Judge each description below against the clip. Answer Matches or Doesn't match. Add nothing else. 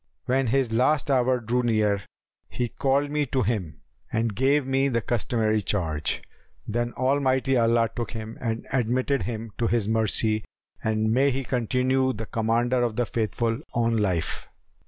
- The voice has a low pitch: Matches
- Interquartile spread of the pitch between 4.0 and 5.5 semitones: Doesn't match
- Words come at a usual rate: Matches